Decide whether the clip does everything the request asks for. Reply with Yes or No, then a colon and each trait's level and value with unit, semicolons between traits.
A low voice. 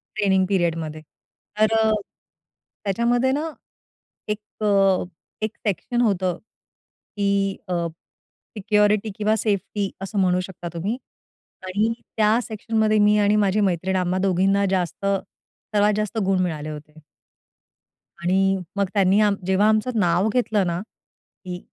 No: high, 200 Hz